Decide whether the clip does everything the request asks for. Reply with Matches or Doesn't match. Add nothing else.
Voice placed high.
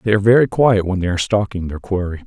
Doesn't match